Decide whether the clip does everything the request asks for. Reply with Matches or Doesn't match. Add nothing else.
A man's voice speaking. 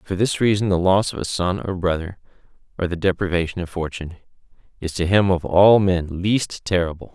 Matches